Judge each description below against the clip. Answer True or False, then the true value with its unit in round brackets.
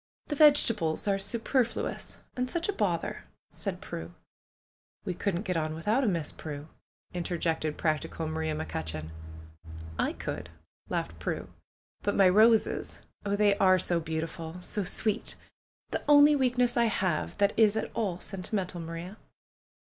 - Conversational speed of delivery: True (150 wpm)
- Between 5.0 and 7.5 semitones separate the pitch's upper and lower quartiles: True (5.5 semitones)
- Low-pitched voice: False (185 Hz)